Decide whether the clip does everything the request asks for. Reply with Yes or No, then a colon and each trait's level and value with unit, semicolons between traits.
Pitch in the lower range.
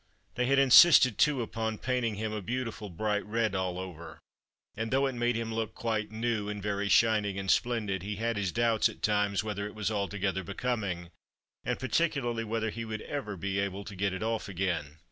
Yes: low, 110 Hz